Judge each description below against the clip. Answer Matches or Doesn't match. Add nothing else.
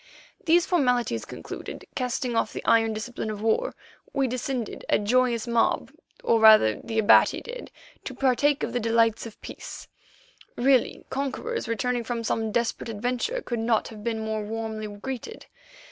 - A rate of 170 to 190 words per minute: Doesn't match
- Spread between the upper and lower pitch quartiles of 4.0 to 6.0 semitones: Doesn't match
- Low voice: Doesn't match